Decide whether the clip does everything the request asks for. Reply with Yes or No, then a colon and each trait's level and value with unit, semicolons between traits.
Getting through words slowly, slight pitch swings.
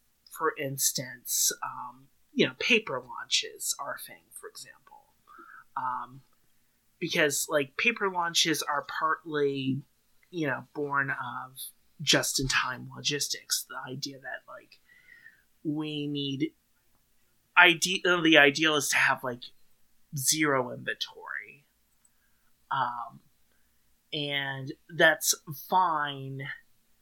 No: slow, 95 wpm; average, 4.4 semitones